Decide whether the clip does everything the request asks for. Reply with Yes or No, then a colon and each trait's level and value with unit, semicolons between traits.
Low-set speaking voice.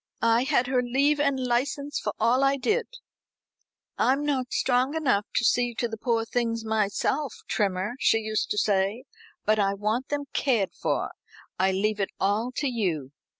No: high, 240 Hz